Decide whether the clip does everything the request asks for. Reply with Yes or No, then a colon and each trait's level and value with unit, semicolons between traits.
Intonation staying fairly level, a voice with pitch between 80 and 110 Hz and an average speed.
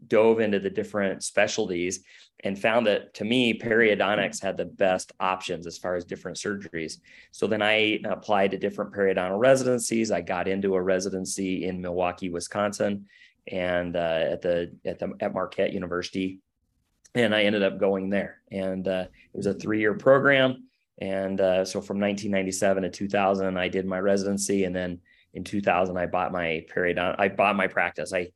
Yes: narrow, 1.9 semitones; very low, 95 Hz; average, 175 wpm